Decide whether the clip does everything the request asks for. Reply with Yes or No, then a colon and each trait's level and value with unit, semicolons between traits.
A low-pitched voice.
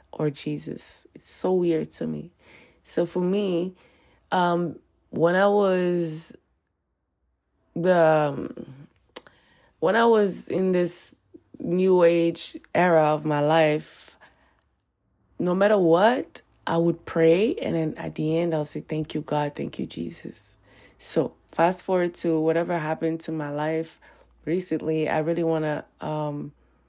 No: medium, 160 Hz